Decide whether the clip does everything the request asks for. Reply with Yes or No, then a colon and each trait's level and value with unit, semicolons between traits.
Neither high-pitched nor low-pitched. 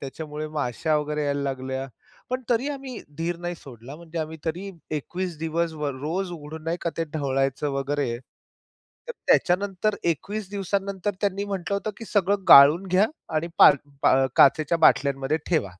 Yes: medium, 165 Hz